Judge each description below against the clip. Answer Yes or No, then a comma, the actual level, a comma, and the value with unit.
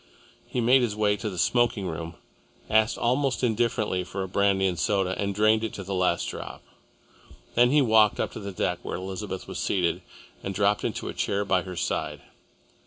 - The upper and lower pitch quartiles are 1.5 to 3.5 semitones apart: Yes, average, 2.9 semitones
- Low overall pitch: Yes, low, 100 Hz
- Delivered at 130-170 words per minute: No, average, 195 wpm